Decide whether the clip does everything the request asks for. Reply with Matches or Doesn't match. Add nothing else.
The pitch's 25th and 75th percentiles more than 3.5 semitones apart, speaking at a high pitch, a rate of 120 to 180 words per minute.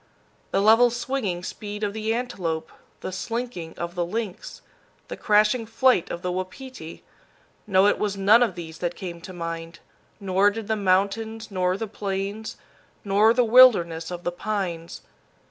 Matches